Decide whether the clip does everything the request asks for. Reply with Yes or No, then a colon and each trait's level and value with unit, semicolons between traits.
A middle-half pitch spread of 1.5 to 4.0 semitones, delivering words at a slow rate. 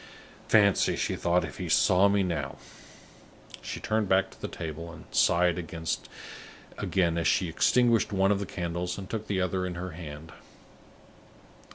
No: average, 2.8 semitones; average, 160 wpm